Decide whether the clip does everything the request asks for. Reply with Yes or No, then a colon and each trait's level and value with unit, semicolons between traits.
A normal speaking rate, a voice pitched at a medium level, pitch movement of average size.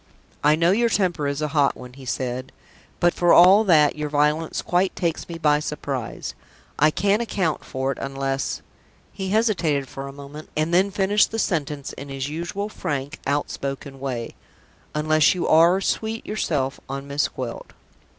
Yes: average, 165 wpm; medium, 150 Hz; average, 4.4 semitones